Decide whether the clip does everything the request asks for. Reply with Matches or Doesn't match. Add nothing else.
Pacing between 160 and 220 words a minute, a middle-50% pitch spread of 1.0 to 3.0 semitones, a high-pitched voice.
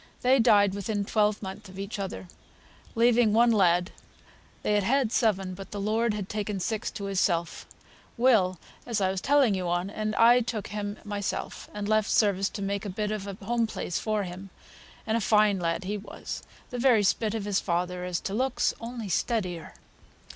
Matches